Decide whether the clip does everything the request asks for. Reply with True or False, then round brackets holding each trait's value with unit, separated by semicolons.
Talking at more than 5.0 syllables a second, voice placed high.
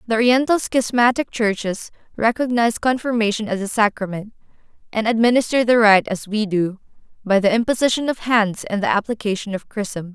True (5.5 syllables/s; 220 Hz)